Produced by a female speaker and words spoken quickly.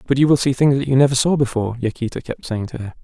No: male; fast, 295 wpm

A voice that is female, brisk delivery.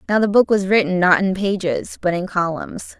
Yes: female; fast, 220 wpm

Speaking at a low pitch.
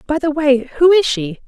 No: very high, 290 Hz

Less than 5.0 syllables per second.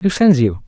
Yes: 4.8 syllables/s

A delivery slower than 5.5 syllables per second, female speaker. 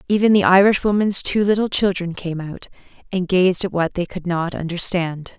Yes: 5.0 syllables/s; female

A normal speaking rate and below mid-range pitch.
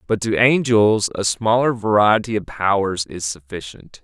Yes: average, 150 wpm; low, 105 Hz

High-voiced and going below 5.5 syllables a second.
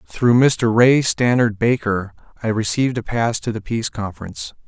No: low, 115 Hz; 5.1 syllables/s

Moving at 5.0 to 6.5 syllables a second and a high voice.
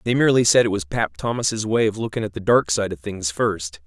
No: 5.6 syllables/s; low, 100 Hz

